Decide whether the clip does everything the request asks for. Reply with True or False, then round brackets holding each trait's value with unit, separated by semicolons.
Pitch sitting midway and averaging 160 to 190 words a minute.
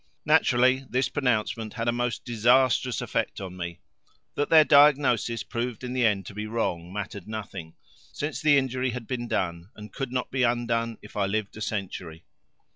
False (115 Hz; 180 wpm)